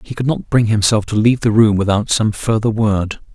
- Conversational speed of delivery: No, fast, 235 wpm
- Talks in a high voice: No, low, 110 Hz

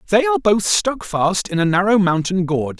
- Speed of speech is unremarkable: No, fast, 215 wpm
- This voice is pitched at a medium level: Yes, medium, 175 Hz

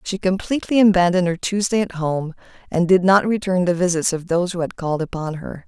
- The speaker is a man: No, female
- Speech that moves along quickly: Yes, fast, 210 wpm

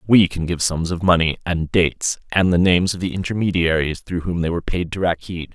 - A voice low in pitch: Yes, very low, 85 Hz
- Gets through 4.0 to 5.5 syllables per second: No, 5.8 syllables/s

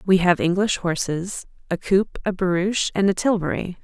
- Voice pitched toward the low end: No, medium, 185 Hz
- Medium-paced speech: Yes, average, 170 wpm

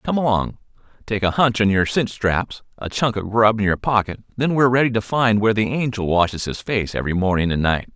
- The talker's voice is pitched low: Yes, low, 105 Hz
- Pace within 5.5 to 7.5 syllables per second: Yes, 5.8 syllables/s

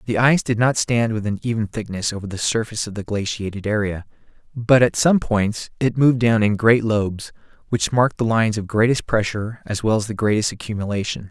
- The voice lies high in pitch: No, low, 110 Hz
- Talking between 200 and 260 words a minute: Yes, fast, 205 wpm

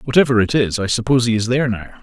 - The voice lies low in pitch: Yes, low, 120 Hz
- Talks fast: Yes, fast, 265 wpm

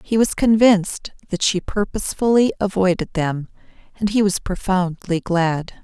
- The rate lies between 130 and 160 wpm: Yes, slow, 135 wpm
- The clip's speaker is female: Yes, female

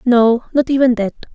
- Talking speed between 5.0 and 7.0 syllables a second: Yes, 5.1 syllables/s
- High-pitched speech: Yes, high, 245 Hz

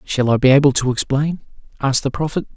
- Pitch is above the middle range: No, medium, 140 Hz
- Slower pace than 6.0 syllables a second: No, 6.5 syllables/s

